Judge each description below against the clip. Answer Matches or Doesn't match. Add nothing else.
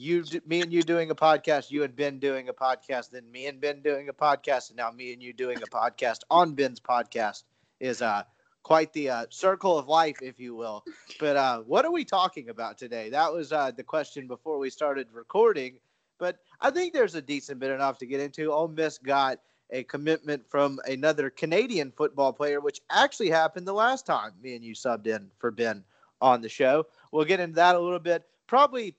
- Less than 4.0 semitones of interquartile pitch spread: Doesn't match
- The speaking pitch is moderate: Matches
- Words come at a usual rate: Doesn't match